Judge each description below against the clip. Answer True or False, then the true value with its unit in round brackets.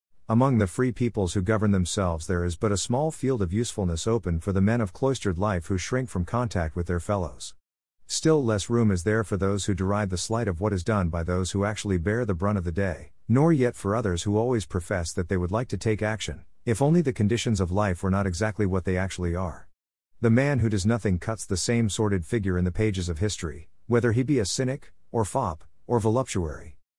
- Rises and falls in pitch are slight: False (4.1 semitones)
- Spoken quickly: True (235 wpm)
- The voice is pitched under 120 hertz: True (105 Hz)